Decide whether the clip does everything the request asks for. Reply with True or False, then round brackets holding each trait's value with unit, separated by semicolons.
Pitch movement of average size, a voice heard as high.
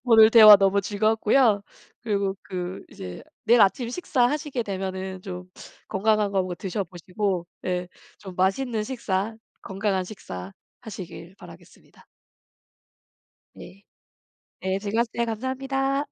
True (3.4 semitones; 200 Hz)